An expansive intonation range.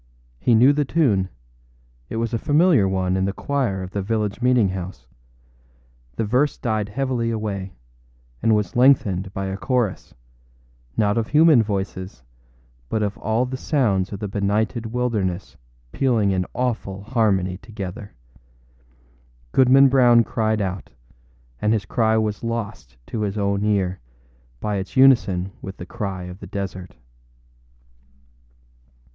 No: average, 3.8 semitones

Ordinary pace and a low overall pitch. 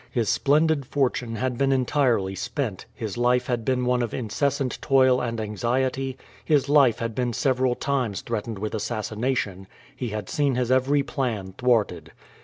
Yes: average, 160 wpm; low, 125 Hz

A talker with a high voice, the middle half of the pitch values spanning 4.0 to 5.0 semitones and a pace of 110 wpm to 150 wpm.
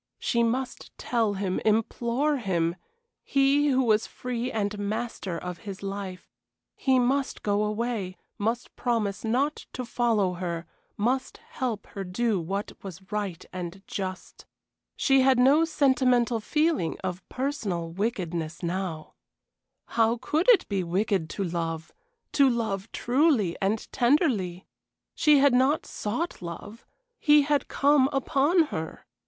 No: high, 225 Hz; wide, 5.6 semitones; slow, 135 wpm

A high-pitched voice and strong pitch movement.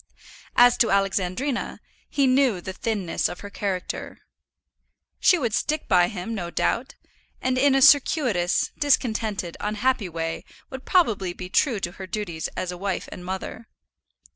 Yes: high, 210 Hz; wide, 5.9 semitones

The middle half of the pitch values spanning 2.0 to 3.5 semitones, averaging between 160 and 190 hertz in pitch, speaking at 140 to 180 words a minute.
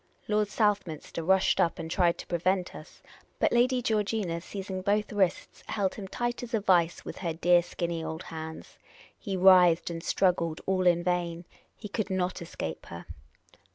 Yes: average, 3.2 semitones; medium, 185 Hz; average, 175 wpm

